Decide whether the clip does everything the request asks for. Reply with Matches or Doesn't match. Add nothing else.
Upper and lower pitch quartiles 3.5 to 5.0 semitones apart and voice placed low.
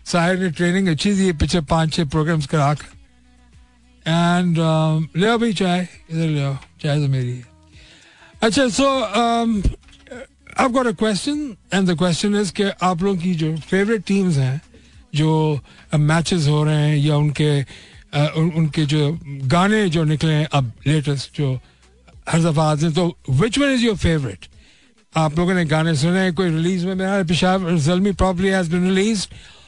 Doesn't match